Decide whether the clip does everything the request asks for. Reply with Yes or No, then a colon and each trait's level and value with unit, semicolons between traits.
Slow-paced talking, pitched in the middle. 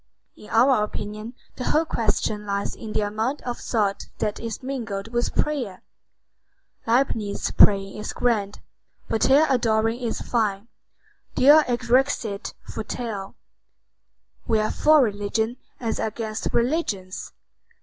No: slow, 120 wpm; high, 225 Hz